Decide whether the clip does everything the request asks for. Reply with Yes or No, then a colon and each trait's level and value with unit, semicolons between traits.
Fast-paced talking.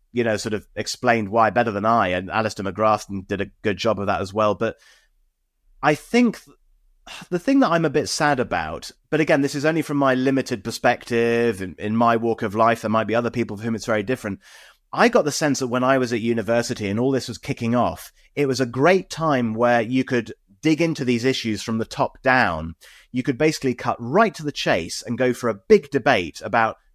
Yes: fast, 230 wpm